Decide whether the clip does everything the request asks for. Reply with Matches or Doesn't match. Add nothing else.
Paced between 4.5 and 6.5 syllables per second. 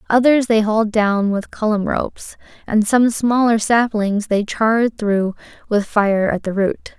Doesn't match